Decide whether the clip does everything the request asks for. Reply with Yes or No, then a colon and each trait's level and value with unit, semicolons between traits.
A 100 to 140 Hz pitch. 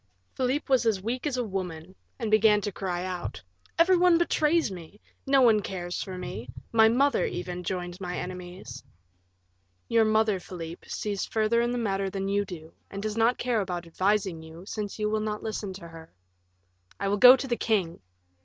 No: high, 205 Hz